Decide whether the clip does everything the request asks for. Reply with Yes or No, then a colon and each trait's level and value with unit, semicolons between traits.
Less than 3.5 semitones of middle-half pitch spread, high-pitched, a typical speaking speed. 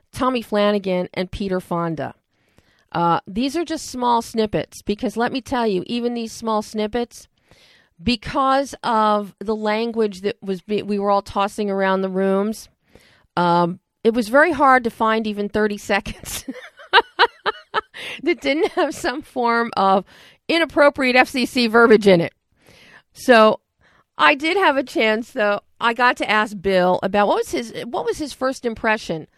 No: average, 4.4 semitones; high, 220 Hz; average, 155 wpm